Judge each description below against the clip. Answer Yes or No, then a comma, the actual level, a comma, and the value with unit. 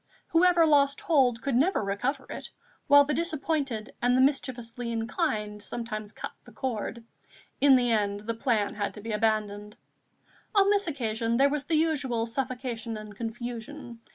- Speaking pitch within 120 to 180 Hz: No, high, 245 Hz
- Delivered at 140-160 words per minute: Yes, average, 155 wpm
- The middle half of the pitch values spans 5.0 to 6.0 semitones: No, average, 4.4 semitones